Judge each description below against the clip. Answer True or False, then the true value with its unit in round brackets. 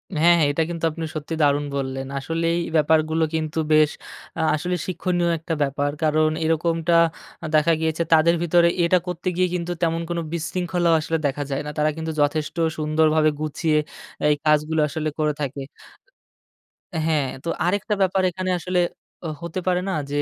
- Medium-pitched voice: True (160 Hz)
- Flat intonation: True (2.0 semitones)